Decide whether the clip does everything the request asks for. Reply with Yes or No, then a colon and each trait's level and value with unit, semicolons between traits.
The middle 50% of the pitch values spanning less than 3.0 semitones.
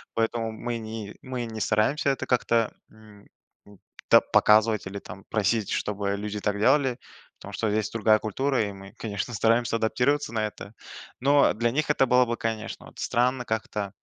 Yes: narrow, 2.5 semitones